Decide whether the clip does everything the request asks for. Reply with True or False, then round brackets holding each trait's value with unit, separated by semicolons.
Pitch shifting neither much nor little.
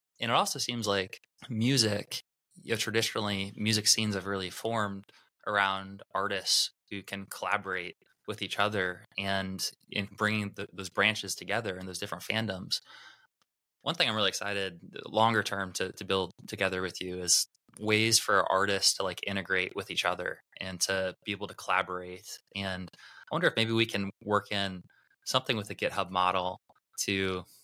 False (2.2 semitones)